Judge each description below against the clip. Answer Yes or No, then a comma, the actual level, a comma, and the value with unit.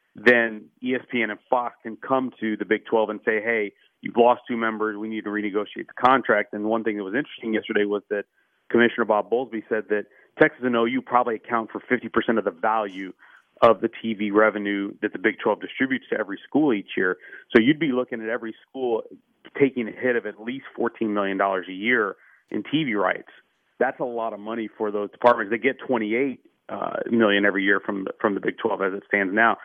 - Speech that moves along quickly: Yes, fast, 215 wpm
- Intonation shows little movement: Yes, narrow, 2.2 semitones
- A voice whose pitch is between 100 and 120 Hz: Yes, low, 110 Hz